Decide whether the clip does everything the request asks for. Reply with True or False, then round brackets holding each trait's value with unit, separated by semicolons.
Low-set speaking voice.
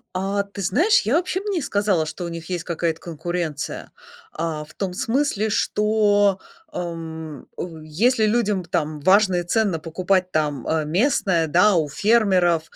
False (180 Hz)